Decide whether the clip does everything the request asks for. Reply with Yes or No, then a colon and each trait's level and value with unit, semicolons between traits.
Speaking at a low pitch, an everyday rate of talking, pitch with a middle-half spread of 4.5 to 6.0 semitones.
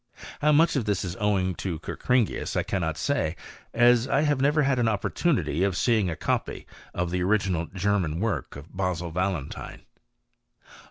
Yes: low, 100 Hz; average, 165 wpm; wide, 5.6 semitones